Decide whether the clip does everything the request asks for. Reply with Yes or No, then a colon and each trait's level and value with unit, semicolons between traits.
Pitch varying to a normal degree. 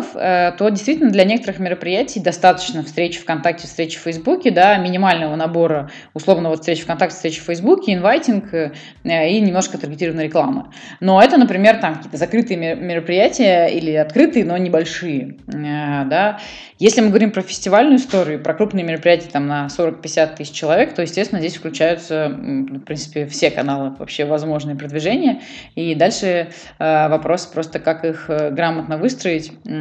Yes: average, 3.5 semitones